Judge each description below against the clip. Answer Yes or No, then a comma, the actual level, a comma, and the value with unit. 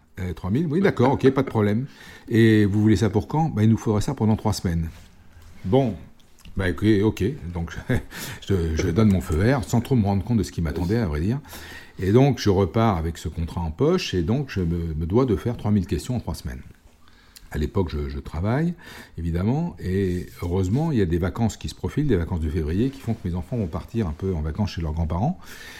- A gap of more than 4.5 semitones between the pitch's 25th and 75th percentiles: Yes, average, 5.0 semitones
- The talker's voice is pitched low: Yes, low, 100 Hz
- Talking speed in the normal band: No, fast, 235 wpm